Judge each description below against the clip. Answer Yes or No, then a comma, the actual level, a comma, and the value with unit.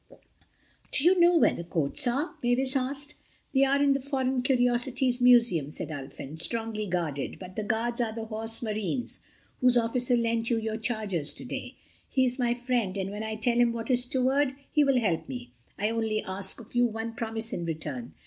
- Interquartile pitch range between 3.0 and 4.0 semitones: Yes, average, 3.4 semitones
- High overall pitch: Yes, high, 230 Hz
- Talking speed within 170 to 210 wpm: Yes, average, 190 wpm